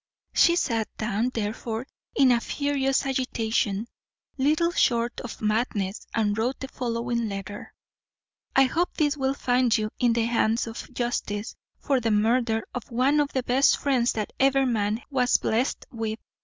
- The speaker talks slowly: No, average, 155 wpm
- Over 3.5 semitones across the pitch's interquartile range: No, average, 3.1 semitones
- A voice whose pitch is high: Yes, high, 240 Hz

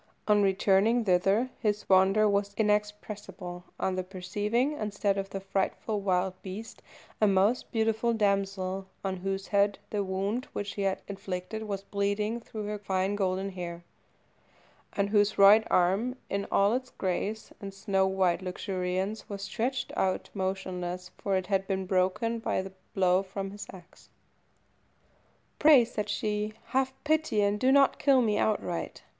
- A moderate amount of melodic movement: No, narrow, 2.1 semitones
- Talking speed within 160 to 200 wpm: No, average, 150 wpm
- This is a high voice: Yes, high, 200 Hz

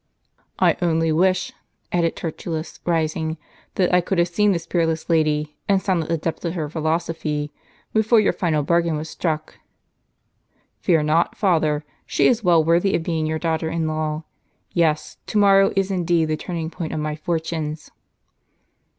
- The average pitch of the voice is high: No, medium, 165 Hz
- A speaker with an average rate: Yes, average, 165 wpm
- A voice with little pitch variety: Yes, narrow, 2.1 semitones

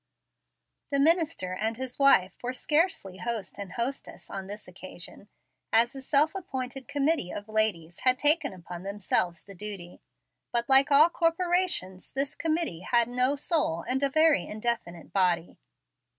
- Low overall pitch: No, high, 240 Hz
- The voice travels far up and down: Yes, wide, 7.1 semitones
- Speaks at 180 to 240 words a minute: No, average, 150 wpm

